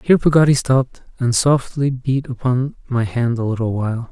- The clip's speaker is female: No, male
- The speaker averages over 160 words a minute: Yes, average, 175 wpm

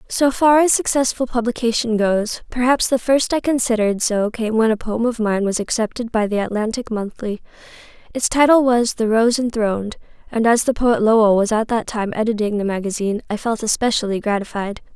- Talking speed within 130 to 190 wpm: Yes, average, 185 wpm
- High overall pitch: Yes, high, 225 Hz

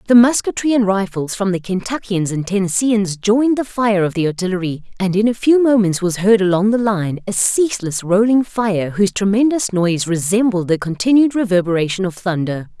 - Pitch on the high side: Yes, high, 200 Hz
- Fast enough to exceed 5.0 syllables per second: Yes, 5.4 syllables/s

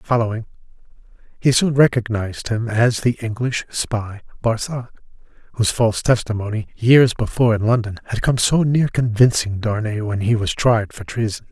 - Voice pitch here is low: Yes, low, 115 Hz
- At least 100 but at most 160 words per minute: Yes, average, 150 wpm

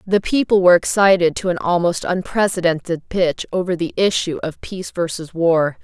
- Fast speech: No, average, 165 wpm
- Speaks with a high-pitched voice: No, medium, 175 Hz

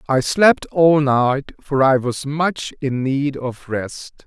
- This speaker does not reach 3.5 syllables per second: Yes, 3.2 syllables/s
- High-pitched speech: No, medium, 140 Hz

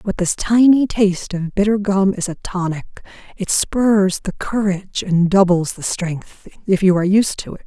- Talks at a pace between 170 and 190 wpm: Yes, average, 180 wpm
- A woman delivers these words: Yes, female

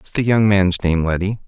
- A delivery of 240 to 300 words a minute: Yes, fast, 245 wpm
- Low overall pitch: Yes, very low, 95 Hz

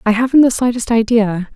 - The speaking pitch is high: Yes, high, 230 Hz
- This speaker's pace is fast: No, average, 195 wpm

